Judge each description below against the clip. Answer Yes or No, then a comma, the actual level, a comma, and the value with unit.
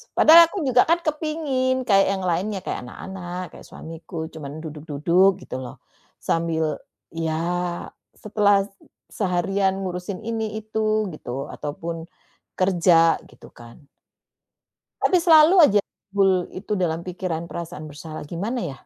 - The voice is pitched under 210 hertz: Yes, medium, 185 Hz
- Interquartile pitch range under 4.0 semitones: No, average, 4.6 semitones